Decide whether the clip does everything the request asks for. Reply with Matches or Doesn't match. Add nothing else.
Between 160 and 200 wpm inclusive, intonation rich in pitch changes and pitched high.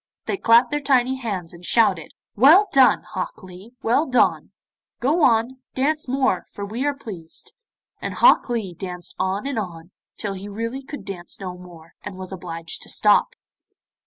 Matches